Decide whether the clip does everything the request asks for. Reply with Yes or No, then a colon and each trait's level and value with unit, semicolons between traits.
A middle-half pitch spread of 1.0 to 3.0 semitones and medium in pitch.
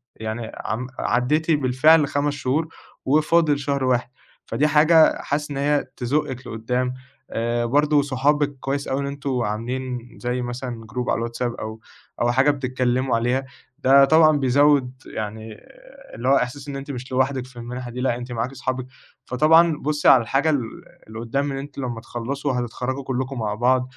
No: average, 2.7 semitones; low, 130 Hz